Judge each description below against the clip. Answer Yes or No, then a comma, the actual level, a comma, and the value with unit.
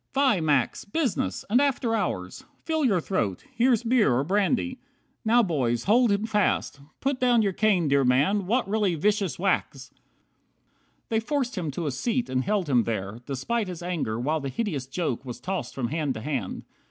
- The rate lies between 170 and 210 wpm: Yes, average, 185 wpm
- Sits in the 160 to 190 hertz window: Yes, medium, 185 Hz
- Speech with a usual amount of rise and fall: No, wide, 8.8 semitones